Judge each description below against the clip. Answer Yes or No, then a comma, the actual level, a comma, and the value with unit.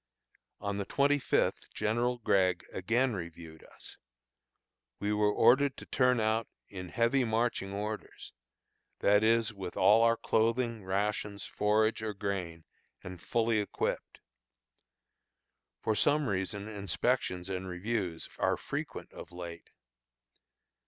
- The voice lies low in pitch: Yes, low, 105 Hz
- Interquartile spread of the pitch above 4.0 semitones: No, average, 3.5 semitones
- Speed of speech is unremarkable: No, slow, 120 wpm